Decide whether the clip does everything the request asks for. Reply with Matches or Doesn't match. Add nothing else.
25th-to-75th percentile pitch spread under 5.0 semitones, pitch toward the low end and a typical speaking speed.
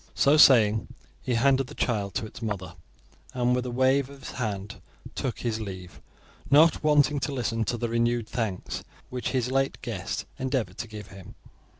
Matches